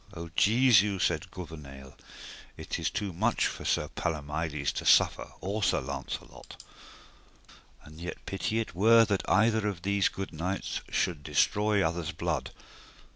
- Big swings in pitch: No, average, 4.3 semitones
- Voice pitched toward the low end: Yes, very low, 90 Hz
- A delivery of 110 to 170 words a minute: Yes, average, 140 wpm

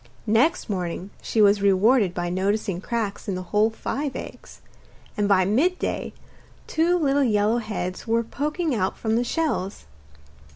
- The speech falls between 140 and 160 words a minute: Yes, average, 150 wpm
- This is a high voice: Yes, high, 215 Hz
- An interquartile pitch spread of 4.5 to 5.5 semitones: Yes, average, 4.9 semitones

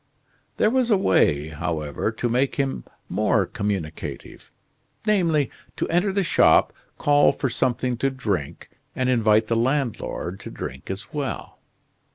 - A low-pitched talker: Yes, low, 120 Hz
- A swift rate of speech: No, average, 140 wpm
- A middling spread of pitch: No, wide, 6.9 semitones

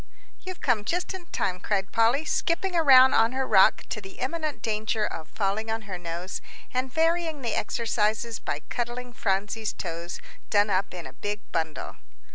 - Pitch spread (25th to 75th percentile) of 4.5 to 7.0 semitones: Yes, average, 5.2 semitones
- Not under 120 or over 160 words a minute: No, average, 170 wpm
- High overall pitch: Yes, high, 220 Hz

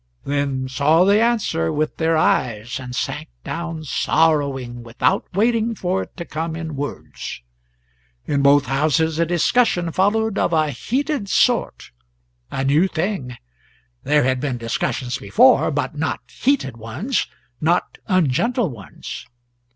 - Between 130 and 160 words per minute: Yes, slow, 135 wpm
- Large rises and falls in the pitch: Yes, wide, 6.3 semitones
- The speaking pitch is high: No, medium, 155 Hz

